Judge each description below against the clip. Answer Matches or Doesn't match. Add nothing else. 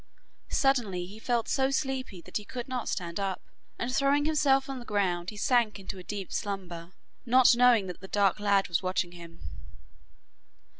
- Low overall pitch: Doesn't match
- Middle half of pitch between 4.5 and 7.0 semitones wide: Matches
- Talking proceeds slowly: Doesn't match